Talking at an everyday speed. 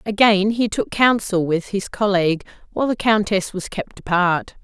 Yes: average, 170 wpm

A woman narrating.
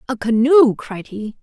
Yes: female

